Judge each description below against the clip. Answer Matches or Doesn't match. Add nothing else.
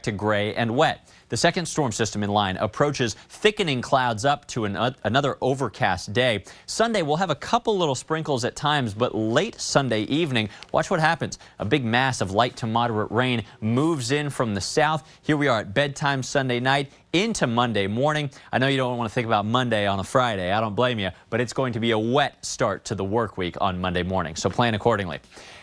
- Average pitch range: Matches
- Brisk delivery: Matches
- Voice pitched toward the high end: Doesn't match